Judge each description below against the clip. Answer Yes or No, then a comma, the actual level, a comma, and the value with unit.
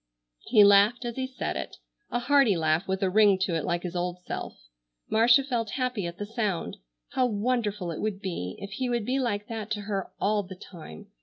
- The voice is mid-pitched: No, high, 205 Hz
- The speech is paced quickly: Yes, fast, 215 wpm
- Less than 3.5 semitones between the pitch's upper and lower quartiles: No, average, 4.2 semitones